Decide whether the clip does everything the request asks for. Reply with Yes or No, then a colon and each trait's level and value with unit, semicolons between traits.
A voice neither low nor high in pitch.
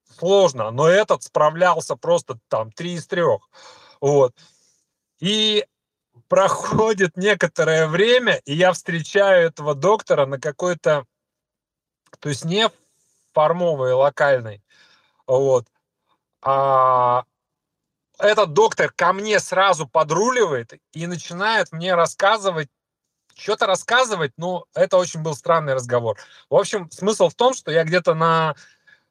Yes: medium, 170 Hz